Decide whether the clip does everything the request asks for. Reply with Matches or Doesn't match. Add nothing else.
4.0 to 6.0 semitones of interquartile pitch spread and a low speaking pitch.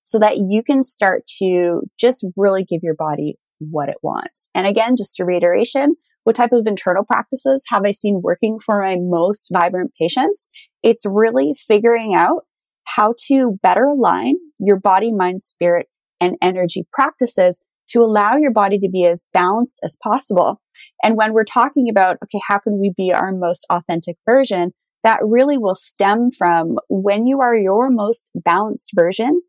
Doesn't match